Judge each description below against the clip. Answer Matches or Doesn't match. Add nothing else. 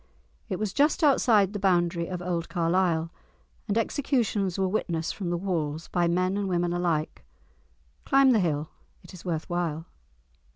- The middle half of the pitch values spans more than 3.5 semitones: Doesn't match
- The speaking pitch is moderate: Matches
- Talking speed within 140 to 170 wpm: Matches